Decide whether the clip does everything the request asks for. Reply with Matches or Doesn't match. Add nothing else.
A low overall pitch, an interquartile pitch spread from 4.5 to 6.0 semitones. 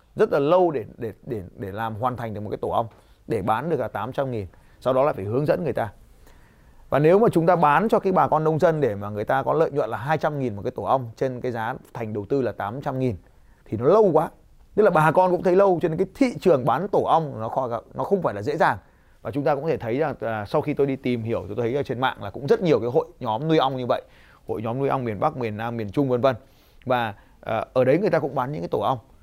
Matches